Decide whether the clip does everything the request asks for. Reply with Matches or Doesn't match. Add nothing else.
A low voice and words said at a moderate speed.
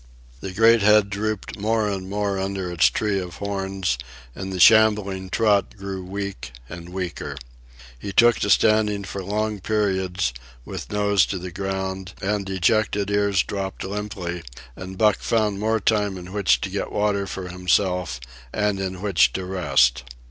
Matches